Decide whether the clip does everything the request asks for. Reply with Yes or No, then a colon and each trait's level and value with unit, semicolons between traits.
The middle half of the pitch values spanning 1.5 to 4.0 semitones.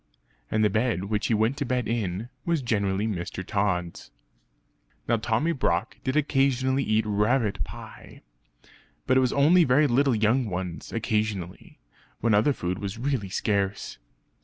No: average, 4.5 semitones